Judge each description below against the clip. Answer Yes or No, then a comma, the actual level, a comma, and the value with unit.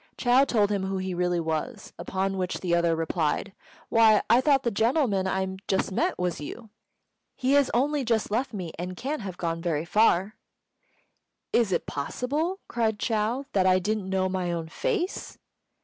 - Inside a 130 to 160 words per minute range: No, average, 175 wpm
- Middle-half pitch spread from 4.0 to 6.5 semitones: Yes, average, 5.0 semitones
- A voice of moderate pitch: No, high, 195 Hz